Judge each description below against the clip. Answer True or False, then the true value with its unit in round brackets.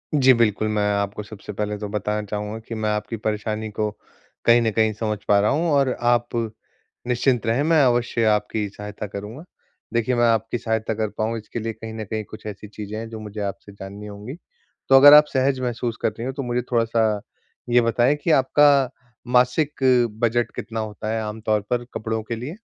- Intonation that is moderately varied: False (2.3 semitones)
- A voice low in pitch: True (110 Hz)